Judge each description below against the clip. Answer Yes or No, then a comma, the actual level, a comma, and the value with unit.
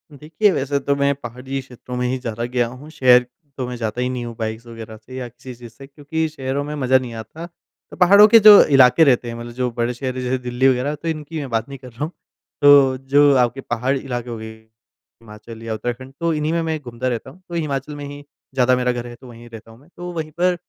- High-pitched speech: No, low, 130 Hz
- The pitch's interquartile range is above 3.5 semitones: No, average, 3.2 semitones